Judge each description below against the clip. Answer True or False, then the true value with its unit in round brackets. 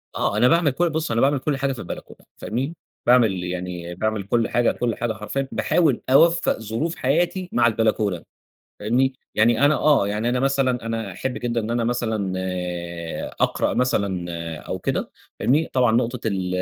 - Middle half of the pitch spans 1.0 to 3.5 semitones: False (4.7 semitones)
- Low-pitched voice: True (120 Hz)